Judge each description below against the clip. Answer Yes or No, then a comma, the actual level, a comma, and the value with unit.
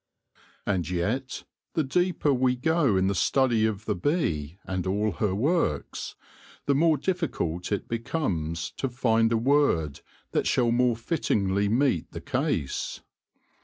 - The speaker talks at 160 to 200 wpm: No, average, 140 wpm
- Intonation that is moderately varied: No, wide, 6.6 semitones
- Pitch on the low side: Yes, low, 115 Hz